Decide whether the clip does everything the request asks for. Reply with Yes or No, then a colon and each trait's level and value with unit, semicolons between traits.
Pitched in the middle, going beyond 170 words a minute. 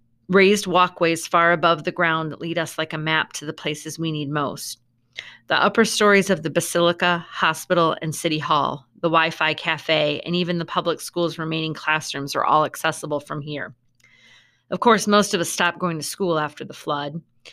Yes: medium, 160 Hz; average, 190 wpm